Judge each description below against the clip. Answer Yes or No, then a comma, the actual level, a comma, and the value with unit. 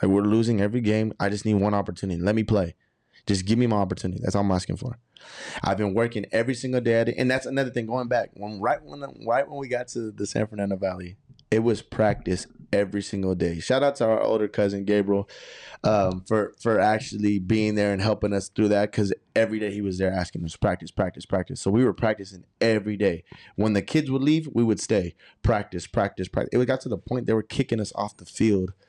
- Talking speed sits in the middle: No, fast, 235 wpm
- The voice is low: Yes, low, 105 Hz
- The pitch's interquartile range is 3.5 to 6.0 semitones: No, average, 2.8 semitones